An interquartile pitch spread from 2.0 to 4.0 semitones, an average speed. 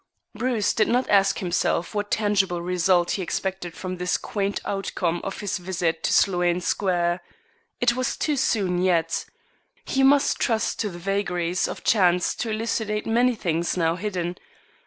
Yes: average, 3.4 semitones; average, 155 wpm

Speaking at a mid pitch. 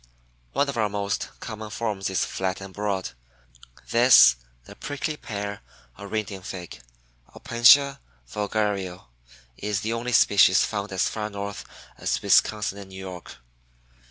No: low, 100 Hz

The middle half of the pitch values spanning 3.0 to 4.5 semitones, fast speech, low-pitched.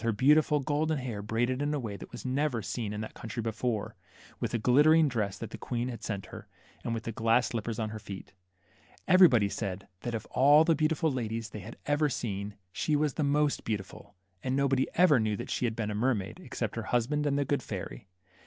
No: average, 4.9 semitones; fast, 225 wpm; low, 120 Hz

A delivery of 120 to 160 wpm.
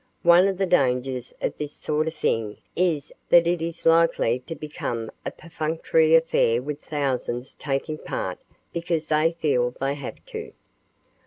Yes: average, 155 wpm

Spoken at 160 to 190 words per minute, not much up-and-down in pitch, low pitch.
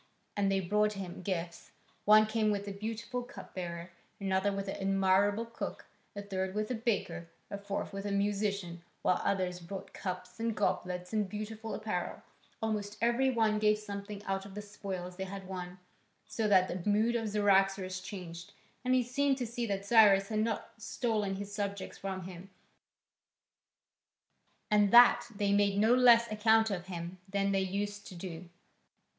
No: average, 170 wpm; narrow, 2.2 semitones; high, 200 Hz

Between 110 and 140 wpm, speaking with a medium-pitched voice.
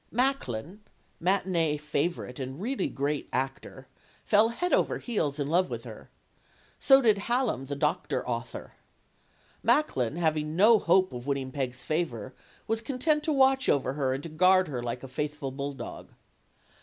No: average, 155 wpm; medium, 155 Hz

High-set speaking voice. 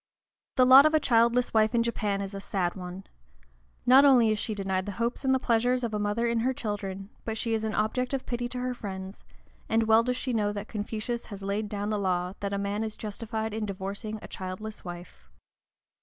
Yes: high, 215 Hz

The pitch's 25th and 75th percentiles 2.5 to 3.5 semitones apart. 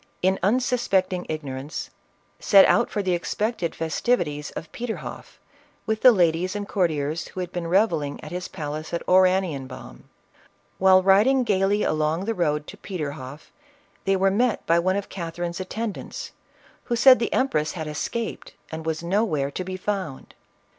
No: average, 4.4 semitones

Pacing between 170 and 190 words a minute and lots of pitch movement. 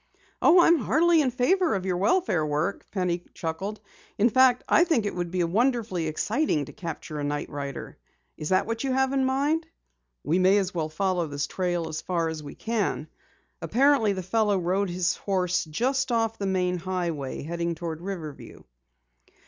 Yes: average, 180 wpm; wide, 6.0 semitones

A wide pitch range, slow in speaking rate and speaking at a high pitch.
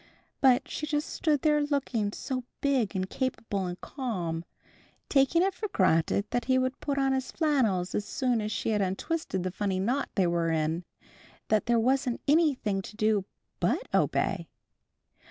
No: wide, 6.3 semitones; average, 170 wpm; high, 240 Hz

